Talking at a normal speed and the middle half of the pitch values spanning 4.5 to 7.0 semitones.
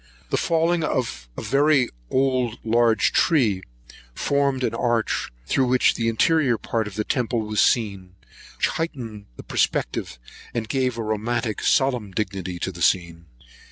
No: average, 150 wpm; average, 4.0 semitones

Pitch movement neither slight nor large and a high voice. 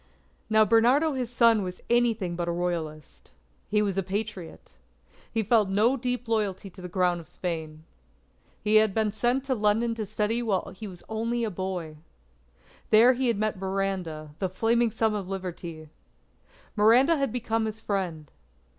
Yes: average, 4.0 semitones; high, 210 Hz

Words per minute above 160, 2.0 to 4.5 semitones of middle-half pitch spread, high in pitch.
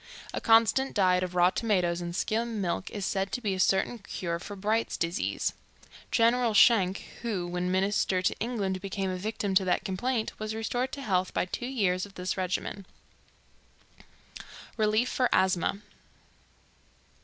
No: average, 155 wpm; average, 3.4 semitones; high, 195 Hz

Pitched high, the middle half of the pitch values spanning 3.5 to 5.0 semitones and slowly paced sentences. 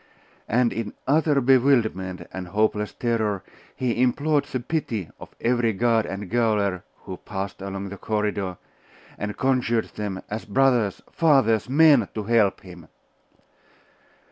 No: low, 110 Hz; average, 4.0 semitones; slow, 130 wpm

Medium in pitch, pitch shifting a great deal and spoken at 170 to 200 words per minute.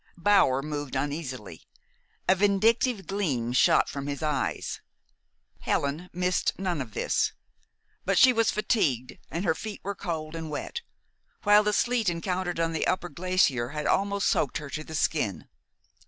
No: medium, 165 Hz; wide, 5.8 semitones; average, 155 wpm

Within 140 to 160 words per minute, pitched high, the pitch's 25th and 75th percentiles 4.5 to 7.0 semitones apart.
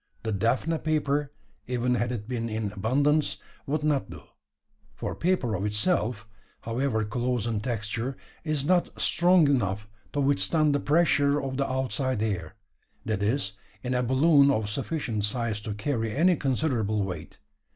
No: average, 150 wpm; low, 125 Hz; average, 4.8 semitones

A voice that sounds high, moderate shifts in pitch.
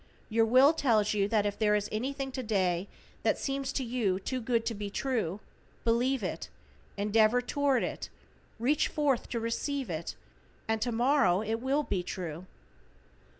Yes: high, 230 Hz; average, 4.2 semitones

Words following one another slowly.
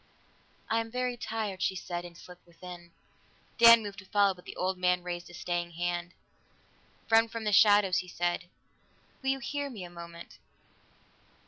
No: average, 175 wpm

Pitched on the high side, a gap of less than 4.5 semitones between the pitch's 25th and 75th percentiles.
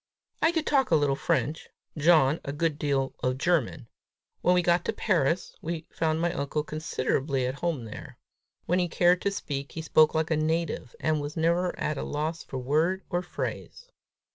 No: medium, 160 Hz; average, 3.4 semitones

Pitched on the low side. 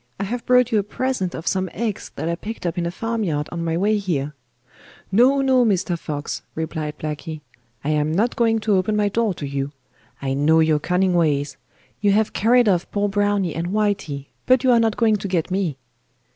No: high, 190 Hz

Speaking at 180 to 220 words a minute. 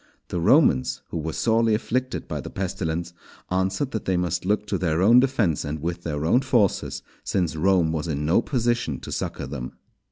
Yes: average, 190 wpm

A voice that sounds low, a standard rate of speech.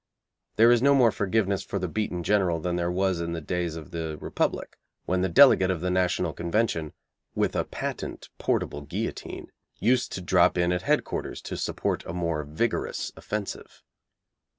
Yes: very low, 90 Hz; average, 175 wpm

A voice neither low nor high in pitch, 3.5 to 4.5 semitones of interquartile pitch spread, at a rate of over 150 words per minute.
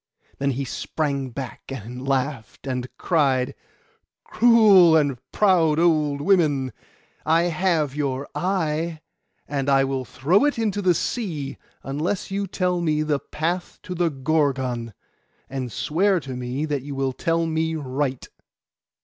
No: medium, 150 Hz; average, 4.2 semitones; slow, 135 wpm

